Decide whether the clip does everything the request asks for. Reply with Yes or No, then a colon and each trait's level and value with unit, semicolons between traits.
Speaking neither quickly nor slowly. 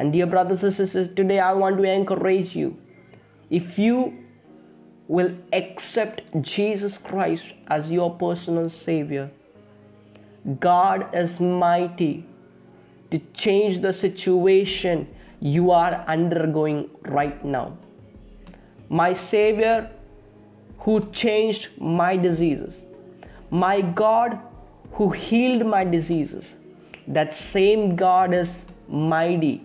No: slow, 100 wpm